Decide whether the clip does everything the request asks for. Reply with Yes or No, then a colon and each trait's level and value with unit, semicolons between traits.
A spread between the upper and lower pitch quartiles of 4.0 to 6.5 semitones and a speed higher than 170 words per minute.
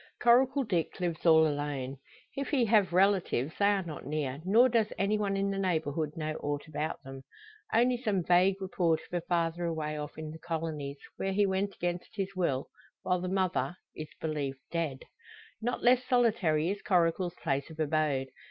Yes: average, 4.3 semitones; average, 180 wpm